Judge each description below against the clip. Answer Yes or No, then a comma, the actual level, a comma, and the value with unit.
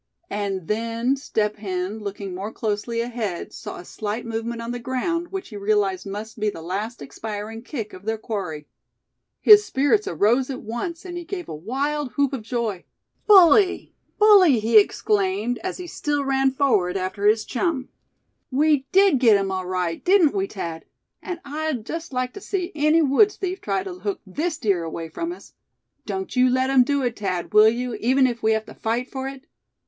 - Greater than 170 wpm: Yes, average, 190 wpm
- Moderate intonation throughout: No, wide, 5.8 semitones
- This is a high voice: Yes, high, 235 Hz